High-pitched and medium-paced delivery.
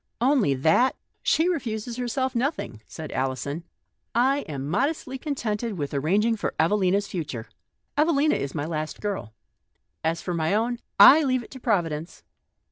Yes: high, 210 Hz; average, 155 wpm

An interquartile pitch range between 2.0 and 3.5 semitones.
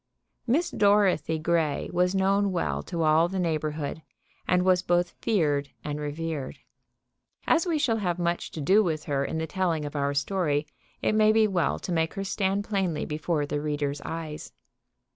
No: average, 4.2 semitones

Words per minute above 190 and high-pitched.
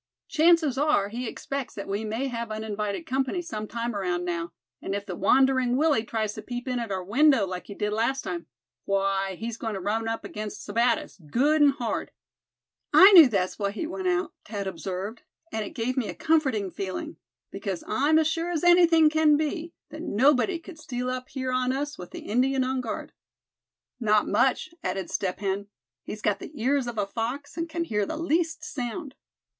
Yes: average, 200 wpm; high, 240 Hz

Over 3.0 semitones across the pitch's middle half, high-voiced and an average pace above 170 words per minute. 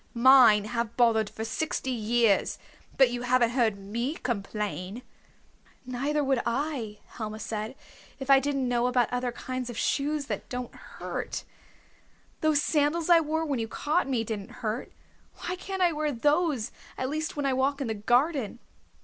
No: average, 4.1 semitones; very high, 250 Hz; average, 165 wpm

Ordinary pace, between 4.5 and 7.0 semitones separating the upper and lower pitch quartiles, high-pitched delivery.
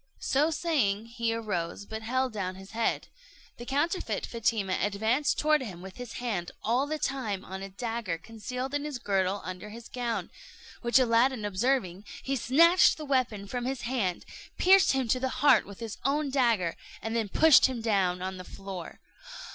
Yes: average, 180 wpm; average, 4.9 semitones; high, 230 Hz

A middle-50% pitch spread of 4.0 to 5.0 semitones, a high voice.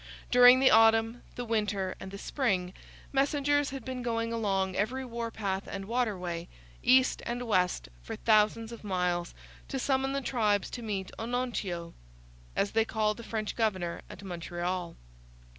Yes: average, 4.4 semitones; high, 220 Hz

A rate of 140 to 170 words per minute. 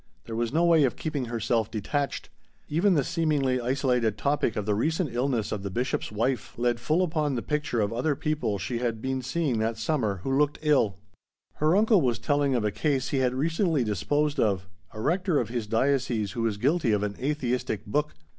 No: average, 200 wpm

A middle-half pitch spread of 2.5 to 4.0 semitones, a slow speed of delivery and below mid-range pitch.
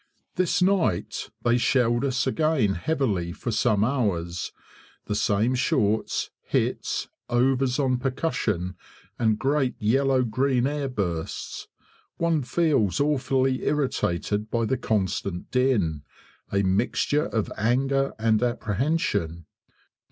No: average, 4.8 semitones; slow, 110 wpm; low, 120 Hz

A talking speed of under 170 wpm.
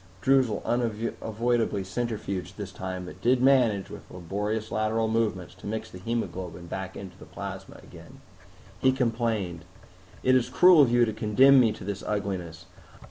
Yes: average, 155 wpm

